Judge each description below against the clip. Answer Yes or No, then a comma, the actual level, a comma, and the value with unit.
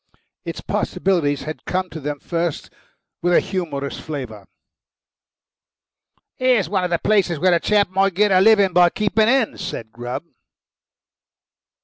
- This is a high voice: No, medium, 180 Hz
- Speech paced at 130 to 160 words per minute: Yes, average, 140 wpm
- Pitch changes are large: No, average, 4.6 semitones